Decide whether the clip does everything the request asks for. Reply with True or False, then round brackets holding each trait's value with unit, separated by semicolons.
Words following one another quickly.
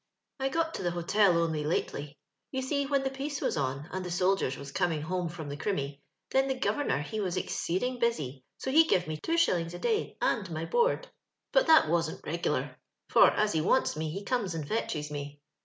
True (220 wpm)